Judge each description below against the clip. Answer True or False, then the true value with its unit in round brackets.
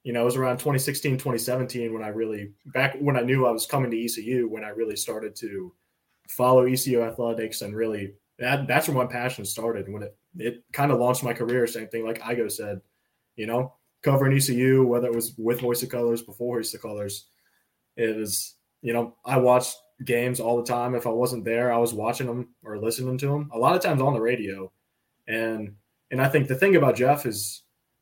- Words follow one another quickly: True (215 wpm)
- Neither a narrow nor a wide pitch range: False (2.1 semitones)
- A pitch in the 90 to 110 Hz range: False (120 Hz)